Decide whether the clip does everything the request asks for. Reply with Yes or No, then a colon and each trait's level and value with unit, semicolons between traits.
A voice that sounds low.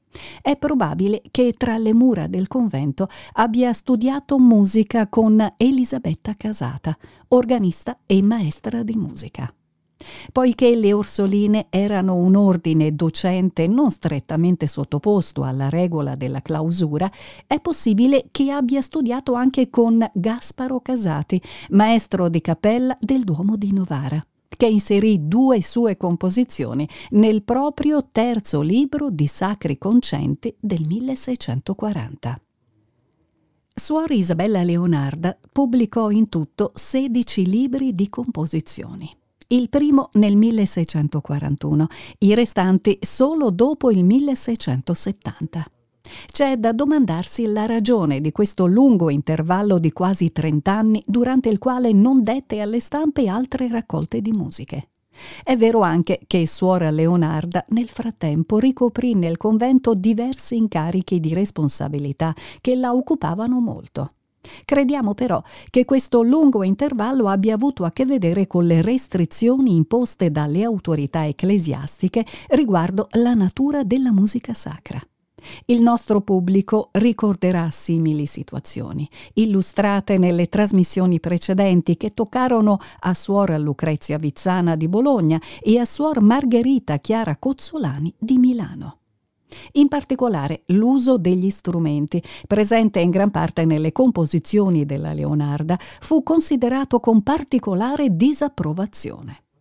No: high, 205 Hz